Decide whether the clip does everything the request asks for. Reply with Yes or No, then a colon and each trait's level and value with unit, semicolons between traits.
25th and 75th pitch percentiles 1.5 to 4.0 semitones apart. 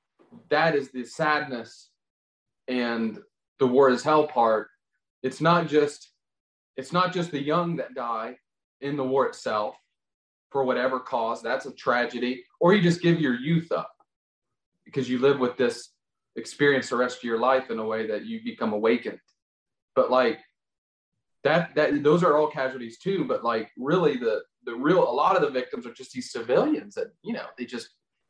No: average, 5.0 semitones